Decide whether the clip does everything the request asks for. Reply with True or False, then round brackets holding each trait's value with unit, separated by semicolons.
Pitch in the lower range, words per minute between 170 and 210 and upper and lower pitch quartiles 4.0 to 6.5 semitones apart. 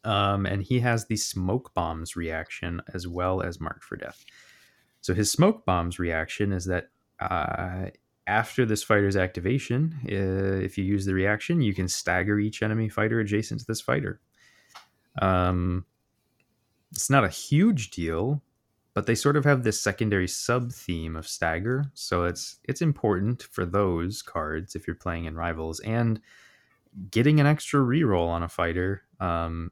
False (100 Hz; 160 wpm; 4.7 semitones)